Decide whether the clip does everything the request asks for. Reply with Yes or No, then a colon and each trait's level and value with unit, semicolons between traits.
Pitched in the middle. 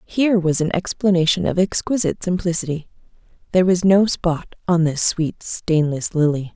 Yes: medium, 175 Hz